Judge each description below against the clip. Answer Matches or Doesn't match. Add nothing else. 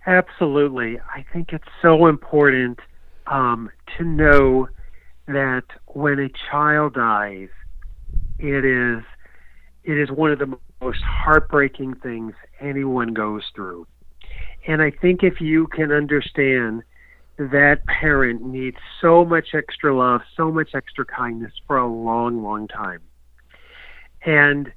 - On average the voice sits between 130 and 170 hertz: Matches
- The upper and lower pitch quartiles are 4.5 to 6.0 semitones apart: Matches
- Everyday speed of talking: Doesn't match